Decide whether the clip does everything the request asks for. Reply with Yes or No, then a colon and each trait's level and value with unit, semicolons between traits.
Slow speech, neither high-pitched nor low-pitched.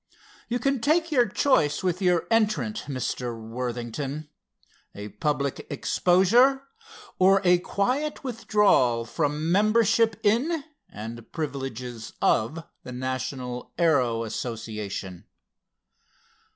Yes: slow, 100 wpm; medium, 150 Hz